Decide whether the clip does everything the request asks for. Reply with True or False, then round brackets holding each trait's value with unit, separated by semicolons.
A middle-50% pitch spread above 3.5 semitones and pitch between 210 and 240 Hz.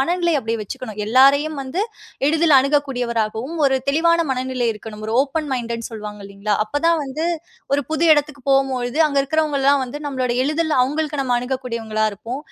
False (4.1 semitones; 265 Hz)